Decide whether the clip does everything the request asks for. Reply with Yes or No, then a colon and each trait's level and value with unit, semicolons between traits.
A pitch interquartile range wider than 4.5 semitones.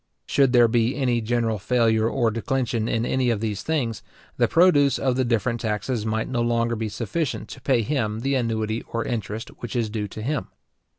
No: average, 2.7 semitones